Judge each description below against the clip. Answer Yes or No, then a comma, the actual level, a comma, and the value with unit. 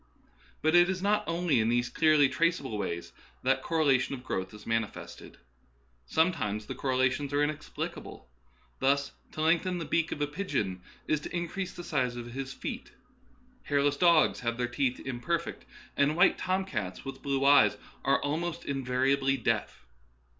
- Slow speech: No, average, 160 wpm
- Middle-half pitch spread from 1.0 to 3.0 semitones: No, average, 4.9 semitones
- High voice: No, medium, 140 Hz